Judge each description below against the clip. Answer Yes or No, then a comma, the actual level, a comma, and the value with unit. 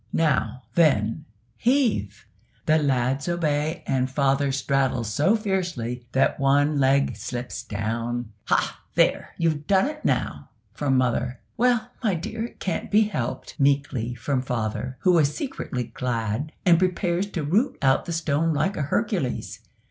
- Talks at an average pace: Yes, average, 145 wpm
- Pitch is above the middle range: No, medium, 140 Hz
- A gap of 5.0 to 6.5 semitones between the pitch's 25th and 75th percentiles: Yes, wide, 5.6 semitones